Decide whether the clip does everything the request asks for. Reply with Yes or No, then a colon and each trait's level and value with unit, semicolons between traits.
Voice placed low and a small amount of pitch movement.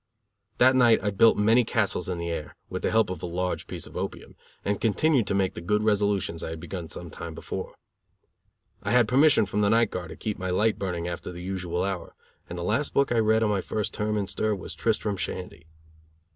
No: low, 100 Hz; average, 3.5 semitones